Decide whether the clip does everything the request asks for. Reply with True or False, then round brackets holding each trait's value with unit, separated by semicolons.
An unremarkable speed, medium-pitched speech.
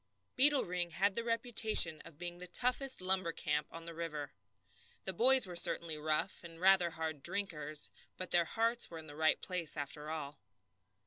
True (180 wpm; 170 Hz)